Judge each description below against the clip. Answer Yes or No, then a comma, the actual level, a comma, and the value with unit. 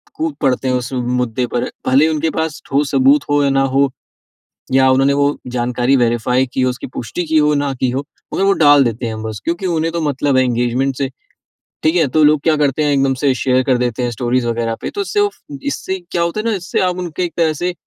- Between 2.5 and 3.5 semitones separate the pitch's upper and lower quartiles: No, average, 4.3 semitones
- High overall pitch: No, low, 135 Hz